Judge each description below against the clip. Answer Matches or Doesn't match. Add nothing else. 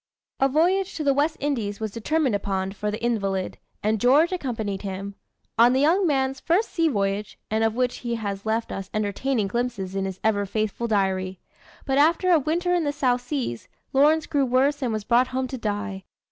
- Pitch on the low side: Doesn't match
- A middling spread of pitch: Doesn't match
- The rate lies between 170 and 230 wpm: Matches